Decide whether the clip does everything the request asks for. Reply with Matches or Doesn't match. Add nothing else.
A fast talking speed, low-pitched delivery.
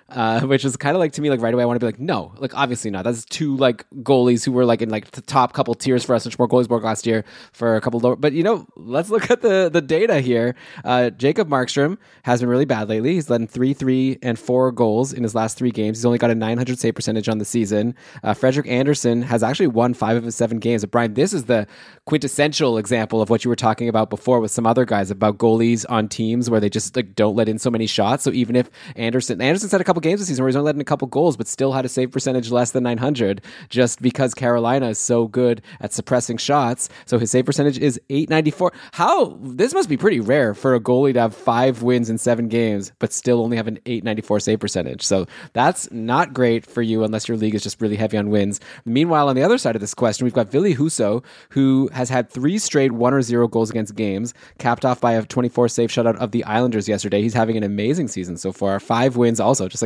Matches